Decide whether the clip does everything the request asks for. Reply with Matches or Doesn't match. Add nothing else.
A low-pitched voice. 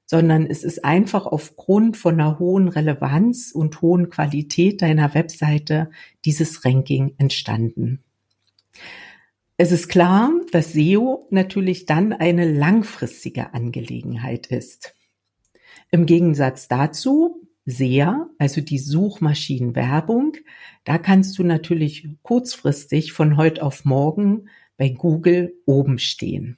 Doesn't match